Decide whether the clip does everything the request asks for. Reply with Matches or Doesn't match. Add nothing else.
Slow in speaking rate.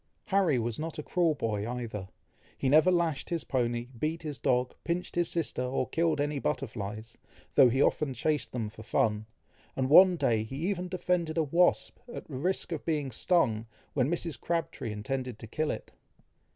Doesn't match